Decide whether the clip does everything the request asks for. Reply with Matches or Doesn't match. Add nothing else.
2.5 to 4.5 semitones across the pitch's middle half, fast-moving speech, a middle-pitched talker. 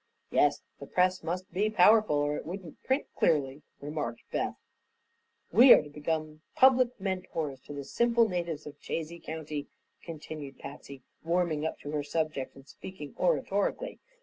Doesn't match